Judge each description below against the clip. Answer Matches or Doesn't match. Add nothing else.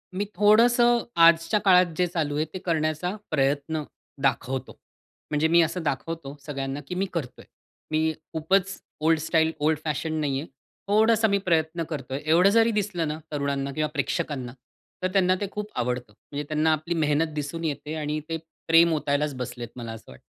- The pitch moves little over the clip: Doesn't match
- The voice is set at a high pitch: Doesn't match